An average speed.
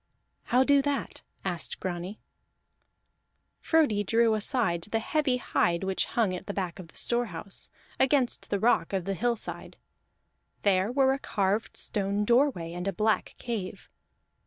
Yes: average, 145 wpm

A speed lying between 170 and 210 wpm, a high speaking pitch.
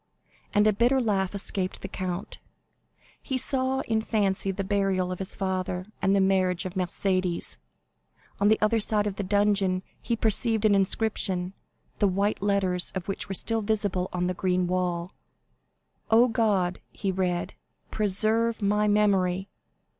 No: average, 155 wpm; high, 195 Hz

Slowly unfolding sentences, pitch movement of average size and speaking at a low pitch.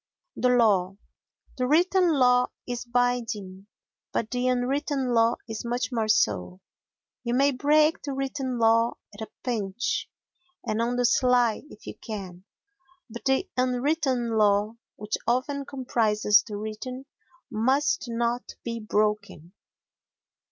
No: slow, 125 wpm; average, 3.1 semitones; high, 240 Hz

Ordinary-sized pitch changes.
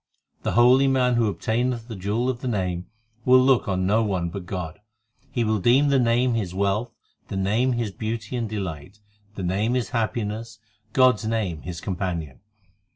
Yes: average, 4.2 semitones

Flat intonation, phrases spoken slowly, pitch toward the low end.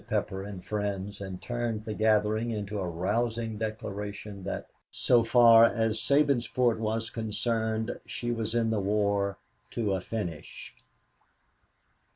Yes: narrow, 2.1 semitones; slow, 130 wpm; low, 110 Hz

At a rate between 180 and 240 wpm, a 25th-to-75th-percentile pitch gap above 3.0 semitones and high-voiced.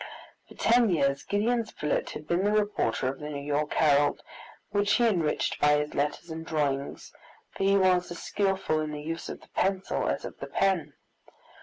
No: average, 190 wpm; average, 5.0 semitones; medium, 165 Hz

